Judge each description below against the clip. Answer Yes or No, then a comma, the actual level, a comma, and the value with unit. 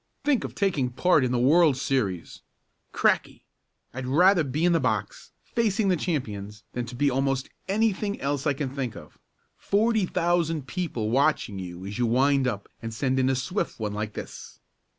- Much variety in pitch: Yes, wide, 6.2 semitones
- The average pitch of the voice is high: No, low, 135 Hz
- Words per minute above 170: Yes, average, 180 wpm